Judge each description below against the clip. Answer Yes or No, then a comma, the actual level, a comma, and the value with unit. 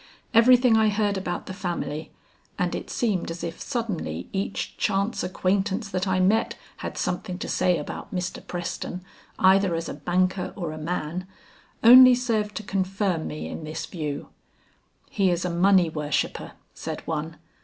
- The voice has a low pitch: No, medium, 185 Hz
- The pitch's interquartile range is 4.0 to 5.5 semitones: No, average, 3.1 semitones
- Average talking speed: Yes, average, 160 wpm